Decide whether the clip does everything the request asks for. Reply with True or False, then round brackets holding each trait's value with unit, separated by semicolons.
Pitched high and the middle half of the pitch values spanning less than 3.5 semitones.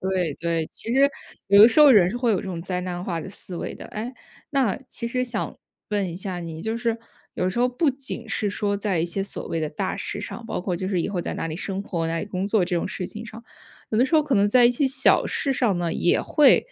False (200 Hz; 5.0 semitones)